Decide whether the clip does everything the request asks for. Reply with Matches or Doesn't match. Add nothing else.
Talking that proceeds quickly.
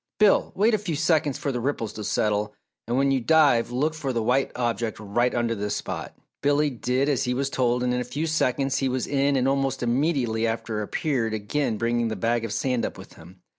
Matches